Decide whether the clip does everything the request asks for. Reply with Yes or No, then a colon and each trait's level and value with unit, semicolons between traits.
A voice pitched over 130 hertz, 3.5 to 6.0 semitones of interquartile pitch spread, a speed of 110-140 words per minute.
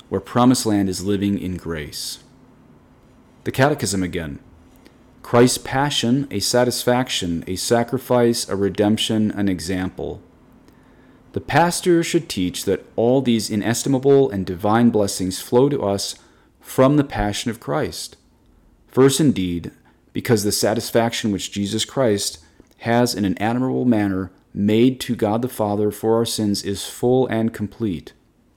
No: low, 110 Hz; average, 3.9 semitones; slow, 135 wpm